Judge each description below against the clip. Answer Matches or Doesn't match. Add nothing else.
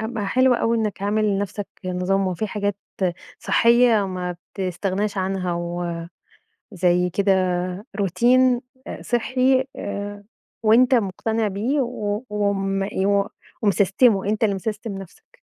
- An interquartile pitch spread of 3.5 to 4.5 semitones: Doesn't match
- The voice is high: Matches